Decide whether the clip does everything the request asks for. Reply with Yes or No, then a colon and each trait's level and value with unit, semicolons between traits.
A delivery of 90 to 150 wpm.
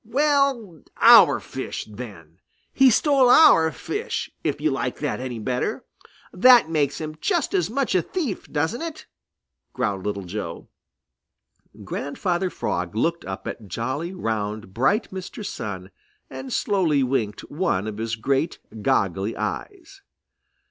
Yes: slow, 135 wpm